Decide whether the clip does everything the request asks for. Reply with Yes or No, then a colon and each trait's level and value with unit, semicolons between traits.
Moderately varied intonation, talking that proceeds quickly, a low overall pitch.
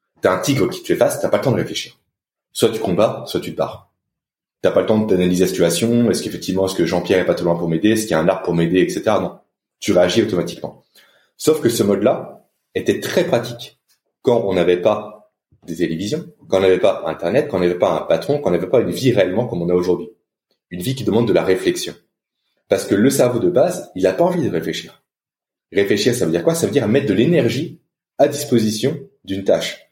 No: wide, 6.7 semitones; fast, 240 wpm; very low, 95 Hz